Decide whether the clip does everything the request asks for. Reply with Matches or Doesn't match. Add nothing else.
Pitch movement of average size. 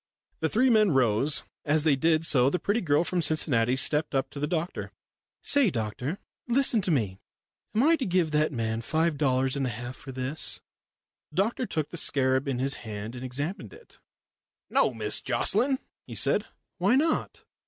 Doesn't match